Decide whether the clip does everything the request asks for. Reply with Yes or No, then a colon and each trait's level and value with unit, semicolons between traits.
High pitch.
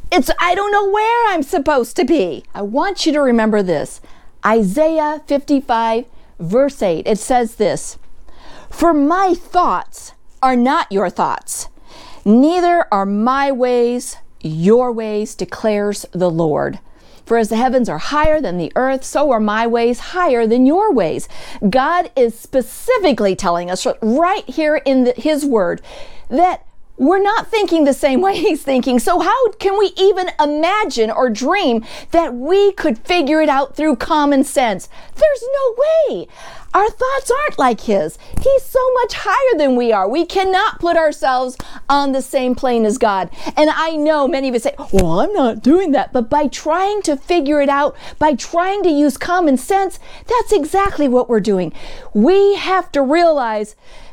Yes: very high, 290 Hz